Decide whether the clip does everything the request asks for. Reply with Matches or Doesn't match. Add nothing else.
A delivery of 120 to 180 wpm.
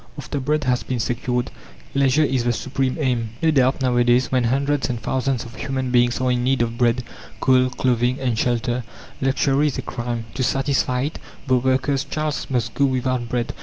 Doesn't match